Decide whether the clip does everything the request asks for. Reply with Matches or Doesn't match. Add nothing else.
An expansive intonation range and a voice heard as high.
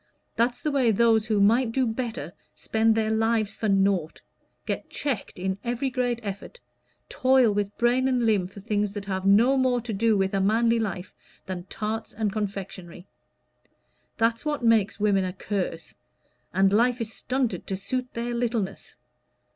Doesn't match